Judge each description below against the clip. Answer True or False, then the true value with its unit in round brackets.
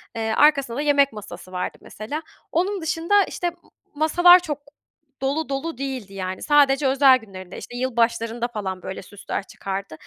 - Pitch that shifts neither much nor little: False (6.0 semitones)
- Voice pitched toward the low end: False (265 Hz)